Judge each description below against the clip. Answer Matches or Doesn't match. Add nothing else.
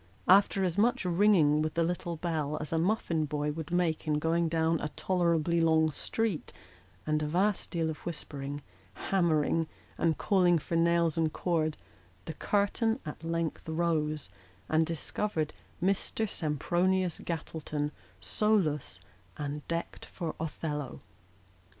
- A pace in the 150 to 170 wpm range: Doesn't match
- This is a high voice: Doesn't match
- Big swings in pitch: Doesn't match